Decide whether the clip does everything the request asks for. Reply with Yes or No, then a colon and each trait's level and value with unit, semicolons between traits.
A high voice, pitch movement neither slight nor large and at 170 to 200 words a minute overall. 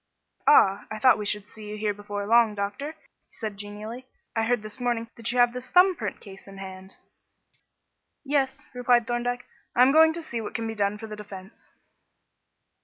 Yes: high, 225 Hz; average, 3.1 semitones; average, 195 wpm